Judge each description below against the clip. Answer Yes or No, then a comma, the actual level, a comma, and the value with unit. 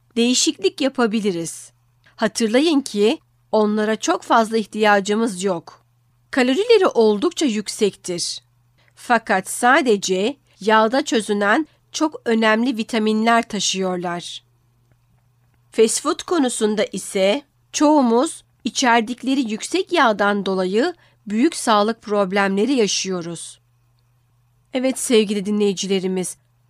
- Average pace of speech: No, slow, 80 wpm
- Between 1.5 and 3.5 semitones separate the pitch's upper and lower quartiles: No, wide, 5.4 semitones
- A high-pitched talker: Yes, high, 210 Hz